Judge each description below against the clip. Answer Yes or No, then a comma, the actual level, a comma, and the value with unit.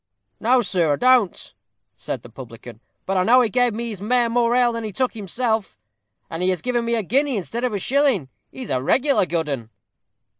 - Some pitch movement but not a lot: No, wide, 5.9 semitones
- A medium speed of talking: No, fast, 210 wpm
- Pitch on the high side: Yes, high, 225 Hz